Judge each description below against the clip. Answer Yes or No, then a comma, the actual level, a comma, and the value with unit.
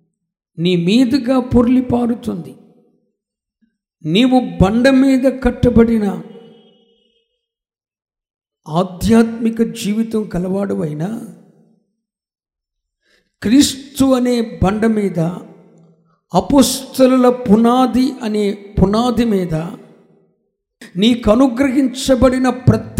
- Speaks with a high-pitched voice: Yes, high, 225 Hz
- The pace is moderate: No, slow, 55 wpm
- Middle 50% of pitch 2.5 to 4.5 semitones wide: No, average, 4.9 semitones